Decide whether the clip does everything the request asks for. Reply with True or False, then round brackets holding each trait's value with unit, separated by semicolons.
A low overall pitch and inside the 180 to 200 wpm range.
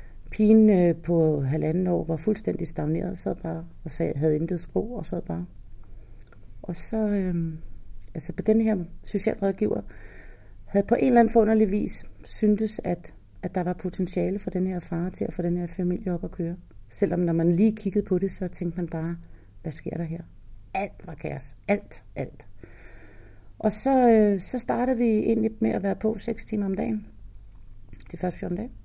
False (180 Hz; 190 wpm)